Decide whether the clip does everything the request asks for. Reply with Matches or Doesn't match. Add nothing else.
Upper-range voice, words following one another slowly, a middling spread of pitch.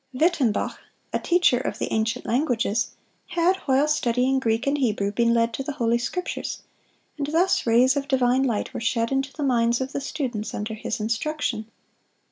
Doesn't match